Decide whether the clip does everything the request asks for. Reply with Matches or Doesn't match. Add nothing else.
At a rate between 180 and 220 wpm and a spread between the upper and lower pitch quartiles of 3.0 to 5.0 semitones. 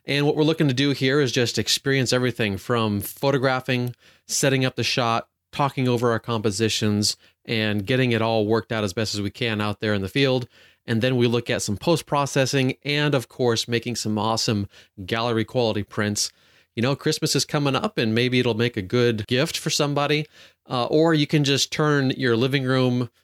Matches